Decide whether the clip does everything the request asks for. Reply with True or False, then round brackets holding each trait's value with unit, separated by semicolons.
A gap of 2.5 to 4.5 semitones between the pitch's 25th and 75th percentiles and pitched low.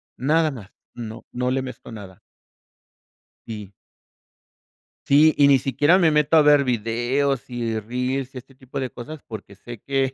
True (3.3 semitones; 130 Hz)